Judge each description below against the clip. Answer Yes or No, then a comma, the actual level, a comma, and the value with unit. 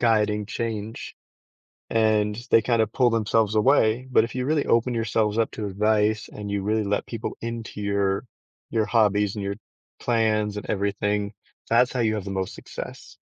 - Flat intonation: Yes, narrow, 1.9 semitones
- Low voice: Yes, low, 110 Hz